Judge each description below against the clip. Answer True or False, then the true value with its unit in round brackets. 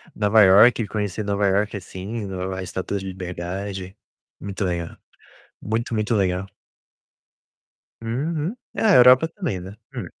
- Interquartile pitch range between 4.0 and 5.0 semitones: False (3.2 semitones)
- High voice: False (100 Hz)